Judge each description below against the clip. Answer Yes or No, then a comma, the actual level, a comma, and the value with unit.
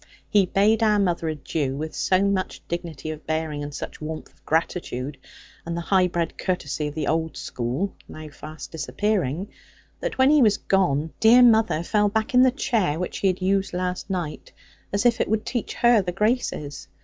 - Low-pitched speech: No, medium, 180 Hz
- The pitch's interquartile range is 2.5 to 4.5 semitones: No, average, 5.1 semitones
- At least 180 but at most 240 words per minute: Yes, average, 190 wpm